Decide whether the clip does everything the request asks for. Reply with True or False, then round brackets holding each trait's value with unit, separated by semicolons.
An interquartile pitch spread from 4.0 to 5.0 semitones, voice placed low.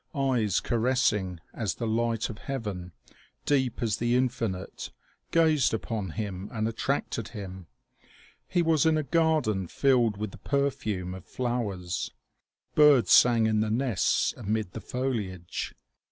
True (4.6 semitones; 115 Hz)